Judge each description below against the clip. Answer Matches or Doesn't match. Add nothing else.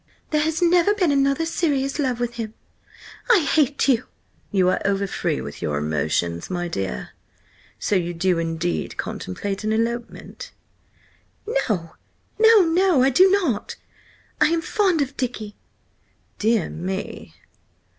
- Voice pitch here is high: Matches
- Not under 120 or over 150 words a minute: Matches